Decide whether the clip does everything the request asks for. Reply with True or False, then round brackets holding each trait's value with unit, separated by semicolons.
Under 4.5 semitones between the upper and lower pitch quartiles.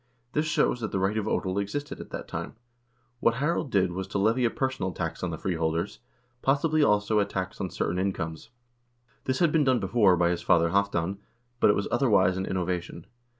False (5.2 semitones)